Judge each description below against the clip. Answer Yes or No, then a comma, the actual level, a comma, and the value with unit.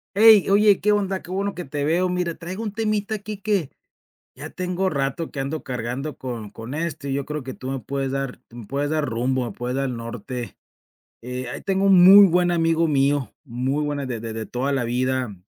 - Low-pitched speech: No, medium, 145 Hz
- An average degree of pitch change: No, wide, 6.1 semitones